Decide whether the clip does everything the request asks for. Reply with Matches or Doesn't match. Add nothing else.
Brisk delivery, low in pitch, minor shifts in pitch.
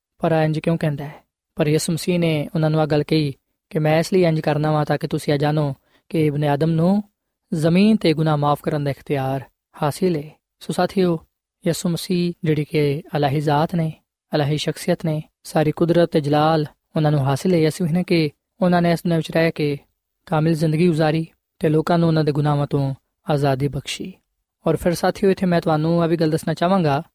Doesn't match